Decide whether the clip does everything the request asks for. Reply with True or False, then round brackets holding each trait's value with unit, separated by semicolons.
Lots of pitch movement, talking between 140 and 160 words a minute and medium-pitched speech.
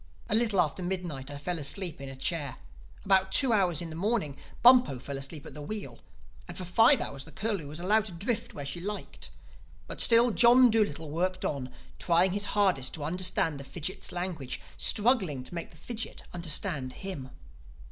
False (6.0 semitones; 185 wpm; 175 Hz)